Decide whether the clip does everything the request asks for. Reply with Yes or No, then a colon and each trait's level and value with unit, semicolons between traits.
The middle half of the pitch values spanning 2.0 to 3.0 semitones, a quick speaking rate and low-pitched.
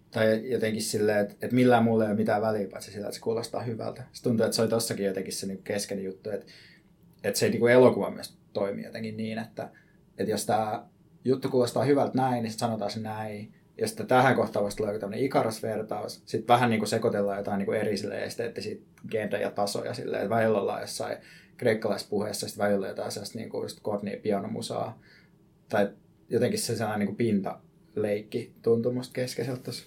Yes: average, 2.7 semitones; fast, 175 wpm; low, 110 Hz